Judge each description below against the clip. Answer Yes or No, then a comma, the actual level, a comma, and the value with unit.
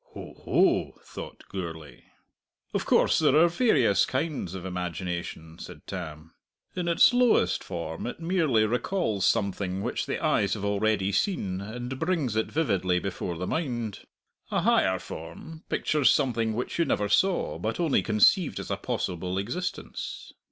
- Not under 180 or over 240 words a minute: No, average, 150 wpm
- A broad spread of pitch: Yes, wide, 9.0 semitones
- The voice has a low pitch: Yes, low, 110 Hz